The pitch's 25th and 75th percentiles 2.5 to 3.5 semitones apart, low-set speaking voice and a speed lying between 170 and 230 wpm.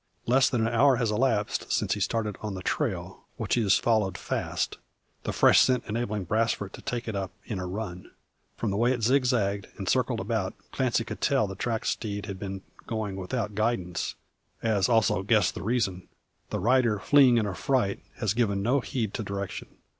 Yes: average, 3.2 semitones; low, 110 Hz; average, 190 wpm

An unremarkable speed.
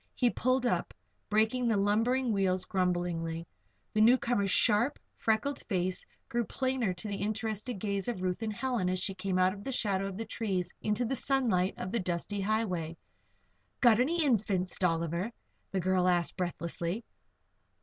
Yes: average, 160 wpm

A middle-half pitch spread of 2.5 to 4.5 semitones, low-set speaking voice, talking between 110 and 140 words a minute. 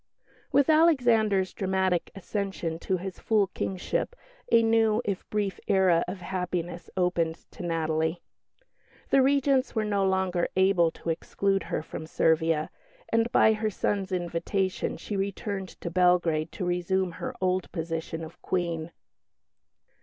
No: average, 3.2 semitones; medium, 185 Hz; slow, 135 wpm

